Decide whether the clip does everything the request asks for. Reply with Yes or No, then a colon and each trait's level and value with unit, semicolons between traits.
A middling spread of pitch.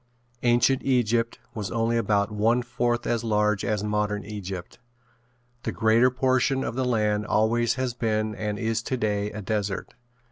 No: narrow, 2.3 semitones